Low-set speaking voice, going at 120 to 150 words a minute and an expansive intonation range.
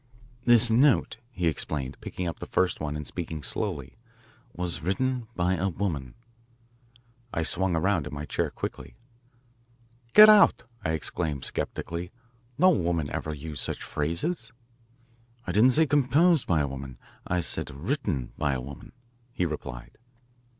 Yes: very low, 85 Hz; average, 145 wpm; wide, 7.2 semitones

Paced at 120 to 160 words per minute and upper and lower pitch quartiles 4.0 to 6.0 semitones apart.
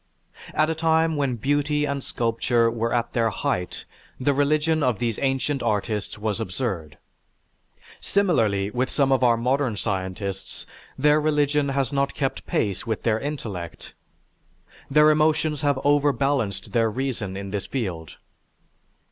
Yes: average, 140 wpm; average, 5.1 semitones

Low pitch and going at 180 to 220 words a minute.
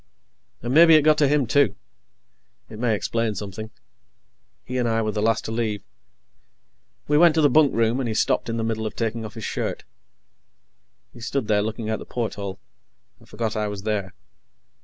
Yes: low, 115 Hz; average, 190 wpm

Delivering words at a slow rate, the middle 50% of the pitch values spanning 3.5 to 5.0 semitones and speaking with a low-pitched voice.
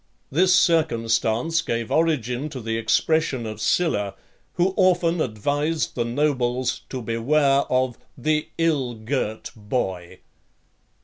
No: slow, 115 wpm; wide, 5.5 semitones; low, 130 Hz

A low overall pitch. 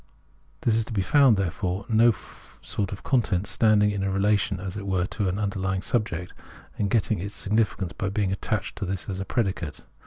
Yes: low, 100 Hz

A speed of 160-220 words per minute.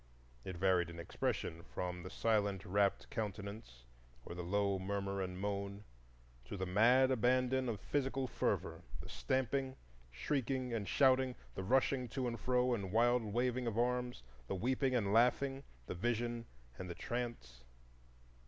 No: average, 145 wpm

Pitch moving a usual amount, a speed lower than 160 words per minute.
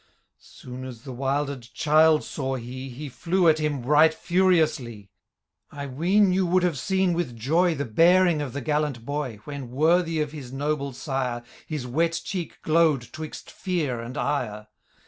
No: average, 4.4 semitones; average, 165 wpm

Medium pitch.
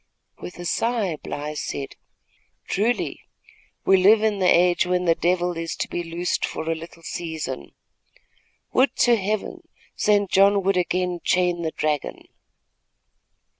Yes: medium, 180 Hz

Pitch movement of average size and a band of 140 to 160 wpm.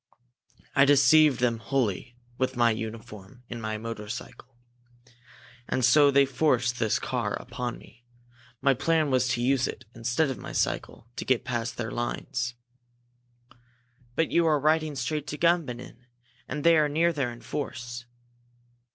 Yes: average, 3.3 semitones; average, 150 wpm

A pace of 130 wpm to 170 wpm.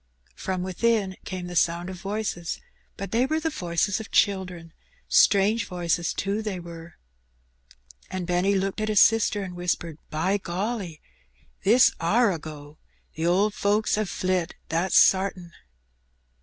Yes: average, 155 wpm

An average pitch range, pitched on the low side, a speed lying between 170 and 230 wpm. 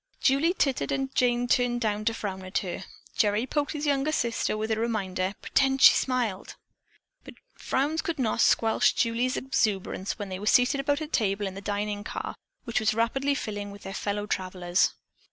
No: average, 4.7 semitones; high, 225 Hz; average, 180 wpm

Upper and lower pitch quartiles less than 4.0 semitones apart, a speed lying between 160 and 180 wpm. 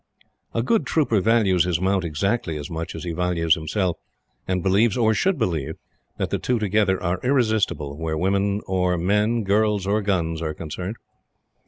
No: average, 4.3 semitones; average, 170 wpm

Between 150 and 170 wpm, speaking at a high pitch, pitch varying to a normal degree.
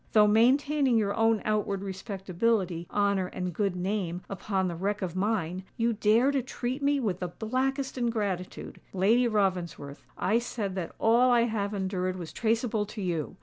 Yes: average, 165 wpm; high, 205 Hz; average, 3.9 semitones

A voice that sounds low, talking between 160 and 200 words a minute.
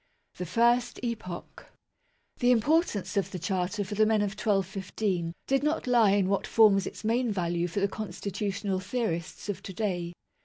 No: high, 200 Hz; average, 165 wpm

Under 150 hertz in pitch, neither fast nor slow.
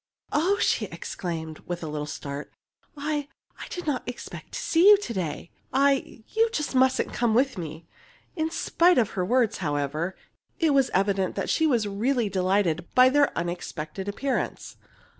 No: high, 220 Hz; average, 160 wpm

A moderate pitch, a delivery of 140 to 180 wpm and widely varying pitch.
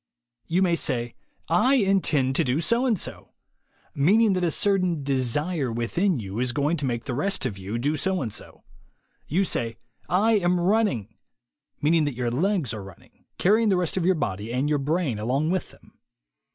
No: medium, 150 Hz; average, 200 wpm; wide, 7.3 semitones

